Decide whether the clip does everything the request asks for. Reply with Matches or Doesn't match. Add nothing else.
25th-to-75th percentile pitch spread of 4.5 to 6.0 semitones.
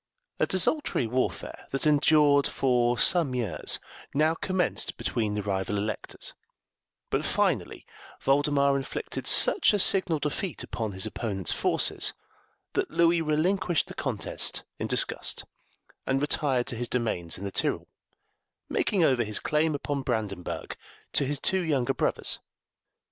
Matches